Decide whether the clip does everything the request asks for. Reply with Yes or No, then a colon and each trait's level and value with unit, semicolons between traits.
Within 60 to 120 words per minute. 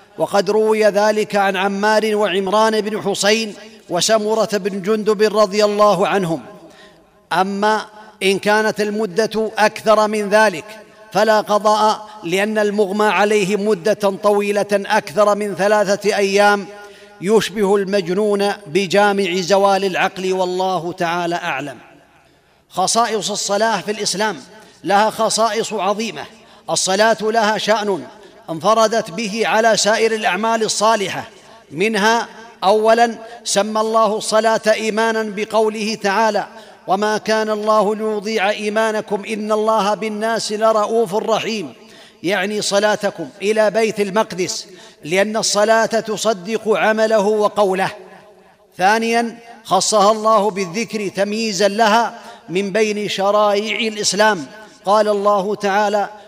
Yes: average, 105 wpm